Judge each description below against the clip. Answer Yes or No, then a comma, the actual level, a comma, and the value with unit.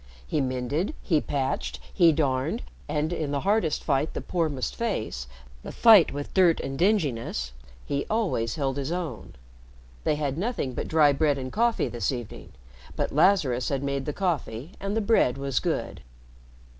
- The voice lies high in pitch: No, medium, 145 Hz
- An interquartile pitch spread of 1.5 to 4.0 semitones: No, average, 5.2 semitones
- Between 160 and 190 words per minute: Yes, average, 170 wpm